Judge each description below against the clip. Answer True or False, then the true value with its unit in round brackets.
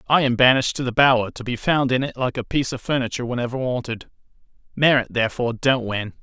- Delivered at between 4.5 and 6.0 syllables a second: False (6.8 syllables/s)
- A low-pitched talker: True (125 Hz)